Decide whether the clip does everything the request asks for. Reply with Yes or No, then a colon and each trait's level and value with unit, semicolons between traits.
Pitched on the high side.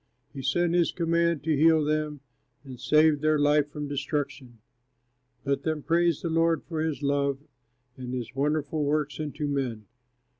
No: medium, 150 Hz